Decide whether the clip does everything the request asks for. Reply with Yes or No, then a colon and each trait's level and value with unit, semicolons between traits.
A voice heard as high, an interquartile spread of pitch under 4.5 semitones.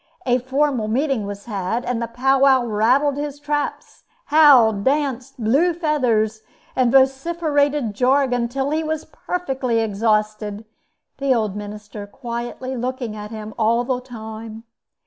Yes: high, 245 Hz; average, 4.0 semitones